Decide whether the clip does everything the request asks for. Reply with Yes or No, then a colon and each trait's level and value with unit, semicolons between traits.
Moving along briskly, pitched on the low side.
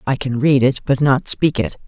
Yes: fast, 255 wpm; low, 130 Hz